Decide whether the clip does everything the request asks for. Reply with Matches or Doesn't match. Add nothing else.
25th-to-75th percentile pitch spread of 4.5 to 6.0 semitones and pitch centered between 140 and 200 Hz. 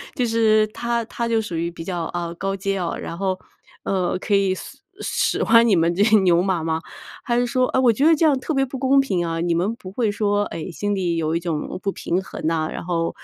Matches